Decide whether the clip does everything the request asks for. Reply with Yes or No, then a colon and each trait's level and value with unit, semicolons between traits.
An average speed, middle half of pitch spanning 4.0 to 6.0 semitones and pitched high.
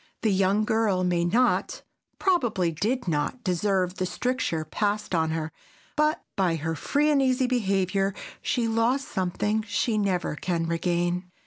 Yes: average, 145 wpm; average, 4.7 semitones; high, 195 Hz